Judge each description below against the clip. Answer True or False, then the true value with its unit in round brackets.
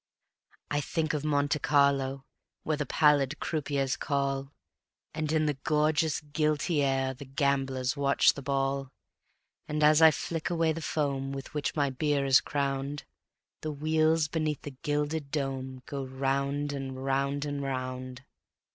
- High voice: False (140 Hz)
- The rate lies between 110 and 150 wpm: True (145 wpm)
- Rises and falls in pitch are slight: True (1.9 semitones)